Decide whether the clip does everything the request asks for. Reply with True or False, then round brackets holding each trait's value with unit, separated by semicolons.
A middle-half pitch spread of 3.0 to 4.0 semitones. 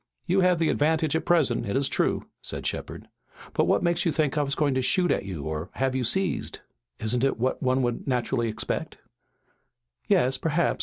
False (4.7 semitones)